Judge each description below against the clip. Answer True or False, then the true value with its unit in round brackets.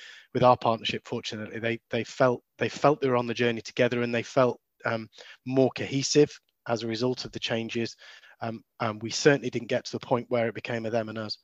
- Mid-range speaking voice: False (120 Hz)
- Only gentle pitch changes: True (1.7 semitones)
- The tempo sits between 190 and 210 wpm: False (225 wpm)